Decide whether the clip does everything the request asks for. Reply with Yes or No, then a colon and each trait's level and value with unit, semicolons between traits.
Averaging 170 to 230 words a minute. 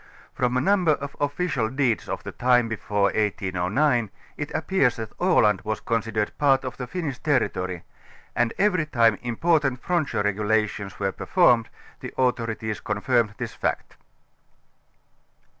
No: average, 140 wpm